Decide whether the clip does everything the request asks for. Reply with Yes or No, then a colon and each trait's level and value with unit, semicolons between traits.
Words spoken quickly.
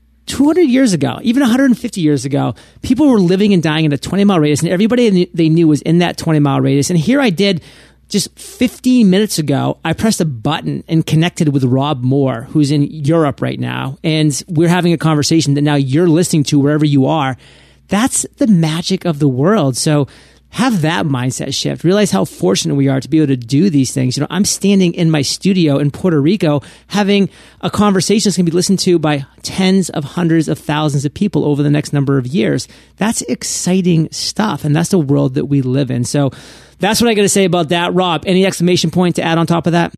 Yes: fast, 220 wpm